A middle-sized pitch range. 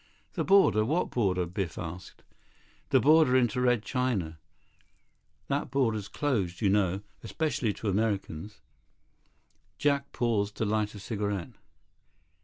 Yes: average, 4.5 semitones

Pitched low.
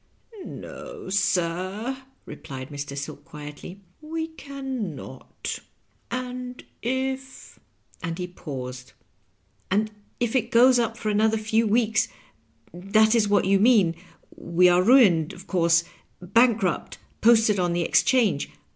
No: high, 205 Hz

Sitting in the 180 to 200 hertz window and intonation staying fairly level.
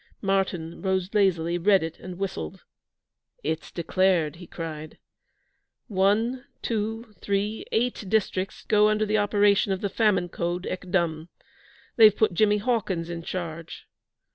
No: high, 190 Hz; average, 3.5 semitones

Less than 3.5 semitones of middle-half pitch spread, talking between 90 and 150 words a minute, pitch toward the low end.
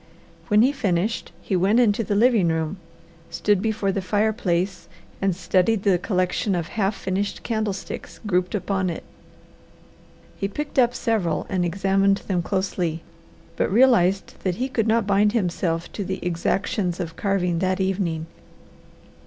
No: average, 2.9 semitones; average, 145 wpm; high, 195 Hz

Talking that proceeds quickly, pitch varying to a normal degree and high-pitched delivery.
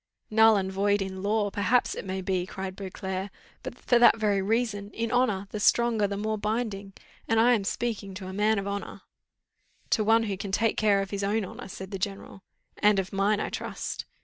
No: fast, 210 wpm; narrow, 2.2 semitones; high, 205 Hz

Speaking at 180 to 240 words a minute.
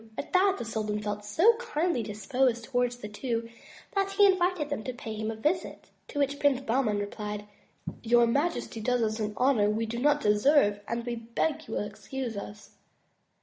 Yes: average, 190 wpm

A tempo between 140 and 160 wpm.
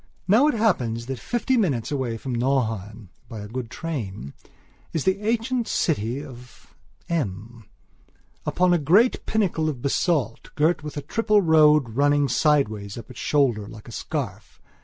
Yes: average, 155 wpm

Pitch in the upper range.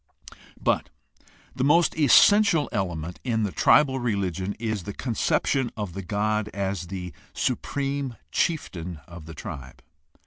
No: low, 105 Hz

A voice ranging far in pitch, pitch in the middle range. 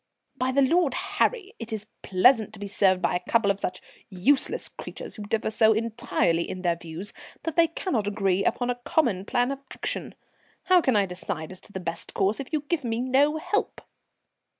No: wide, 6.2 semitones; high, 225 Hz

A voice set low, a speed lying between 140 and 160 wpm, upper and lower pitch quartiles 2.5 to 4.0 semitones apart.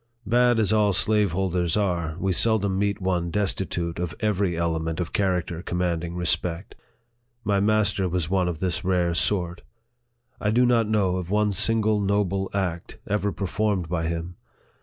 Yes: very low, 95 Hz; average, 155 wpm; average, 3.1 semitones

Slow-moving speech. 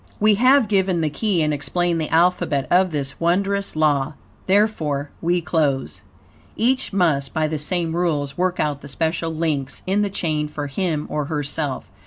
No: average, 170 wpm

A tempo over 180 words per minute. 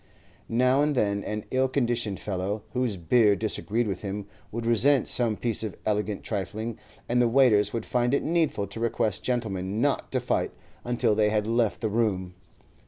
No: average, 175 wpm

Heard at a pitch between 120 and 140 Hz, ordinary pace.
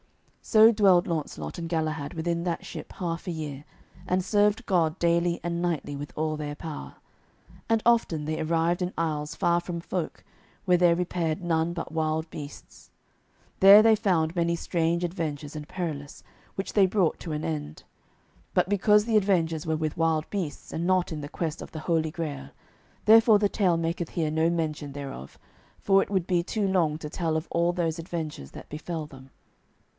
No: medium, 165 Hz; average, 180 wpm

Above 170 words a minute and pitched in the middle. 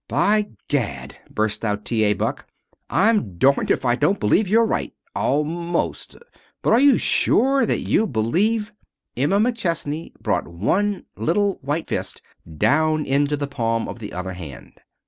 No: average, 155 wpm; medium, 150 Hz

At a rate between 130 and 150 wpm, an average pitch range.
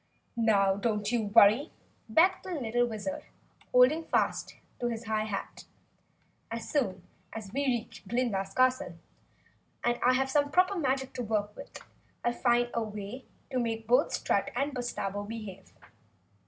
Yes: average, 145 wpm; average, 3.4 semitones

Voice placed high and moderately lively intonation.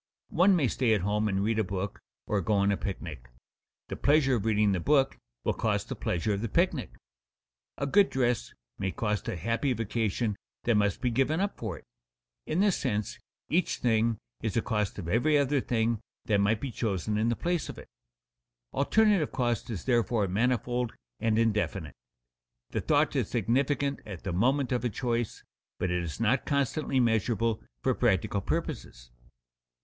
No: low, 115 Hz; average, 4.4 semitones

